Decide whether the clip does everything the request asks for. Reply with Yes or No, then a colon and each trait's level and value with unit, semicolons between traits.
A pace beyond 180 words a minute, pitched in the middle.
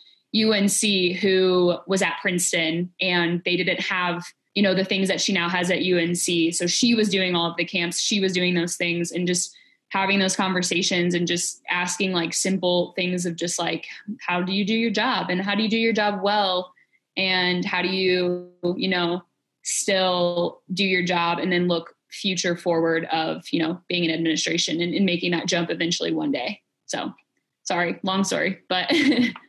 Yes: average, 190 wpm; medium, 180 Hz